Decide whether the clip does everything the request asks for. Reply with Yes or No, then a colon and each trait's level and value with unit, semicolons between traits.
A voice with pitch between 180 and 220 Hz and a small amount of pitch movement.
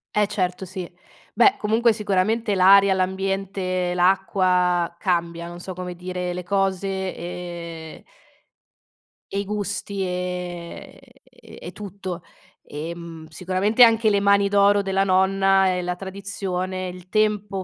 Yes: high, 190 Hz; narrow, 1.8 semitones